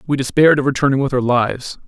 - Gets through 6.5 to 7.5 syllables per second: Yes, 7.1 syllables/s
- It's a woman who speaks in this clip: No, male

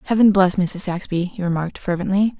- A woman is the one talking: Yes, female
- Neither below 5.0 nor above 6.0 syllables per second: Yes, 5.9 syllables/s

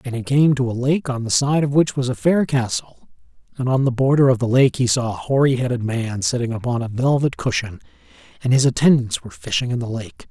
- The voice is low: Yes, low, 125 Hz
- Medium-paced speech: No, fast, 240 wpm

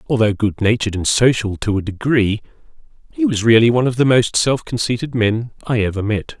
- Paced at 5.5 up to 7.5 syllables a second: Yes, 5.7 syllables/s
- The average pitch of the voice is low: Yes, low, 115 Hz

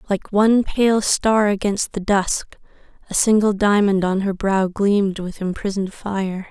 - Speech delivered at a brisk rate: No, average, 155 wpm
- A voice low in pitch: No, high, 200 Hz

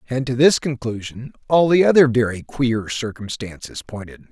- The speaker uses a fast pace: No, average, 155 wpm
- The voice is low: Yes, low, 125 Hz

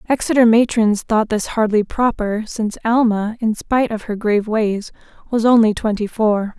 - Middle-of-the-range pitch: No, high, 220 Hz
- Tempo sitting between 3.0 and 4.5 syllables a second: No, 4.9 syllables/s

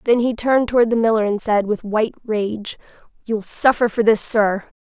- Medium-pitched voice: No, high, 220 Hz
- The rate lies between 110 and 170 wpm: No, average, 200 wpm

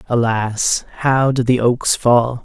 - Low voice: Yes, low, 120 Hz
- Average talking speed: Yes, average, 150 wpm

